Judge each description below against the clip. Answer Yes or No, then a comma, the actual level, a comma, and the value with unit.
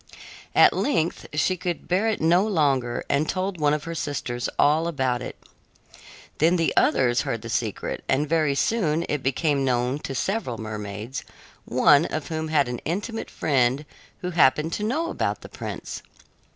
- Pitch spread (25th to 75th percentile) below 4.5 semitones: No, average, 4.9 semitones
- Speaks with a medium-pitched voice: Yes, medium, 150 Hz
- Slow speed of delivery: No, average, 165 wpm